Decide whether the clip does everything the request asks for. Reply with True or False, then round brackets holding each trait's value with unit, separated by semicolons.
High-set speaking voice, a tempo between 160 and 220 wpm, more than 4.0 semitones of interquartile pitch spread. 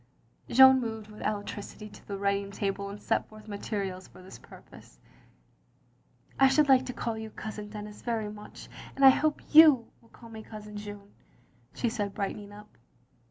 False (210 Hz; 180 wpm; 2.4 semitones)